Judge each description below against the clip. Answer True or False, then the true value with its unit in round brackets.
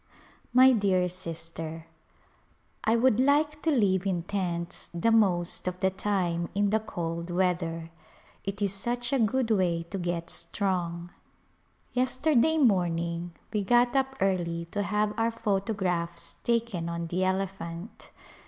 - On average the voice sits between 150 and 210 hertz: True (190 Hz)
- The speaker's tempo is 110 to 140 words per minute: True (135 wpm)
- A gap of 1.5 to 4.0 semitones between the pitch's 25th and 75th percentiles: False (4.8 semitones)